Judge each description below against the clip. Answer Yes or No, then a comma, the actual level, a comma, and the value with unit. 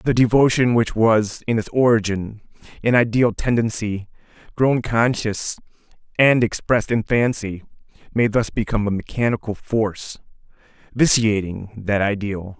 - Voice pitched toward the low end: Yes, low, 110 Hz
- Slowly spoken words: Yes, slow, 120 wpm